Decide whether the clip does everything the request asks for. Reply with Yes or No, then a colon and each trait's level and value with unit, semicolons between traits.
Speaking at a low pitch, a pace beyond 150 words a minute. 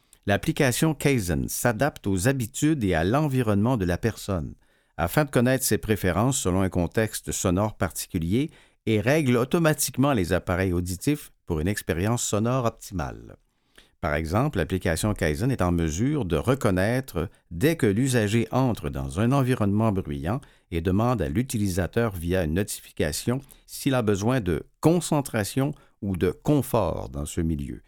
No: low, 110 Hz; slow, 145 wpm